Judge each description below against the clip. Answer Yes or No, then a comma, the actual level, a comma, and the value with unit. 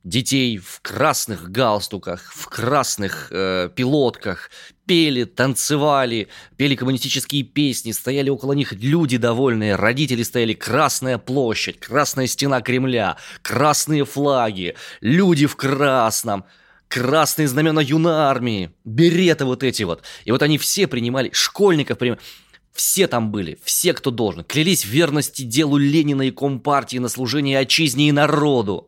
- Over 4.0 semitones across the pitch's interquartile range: No, average, 3.7 semitones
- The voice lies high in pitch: No, low, 135 Hz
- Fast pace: No, average, 130 wpm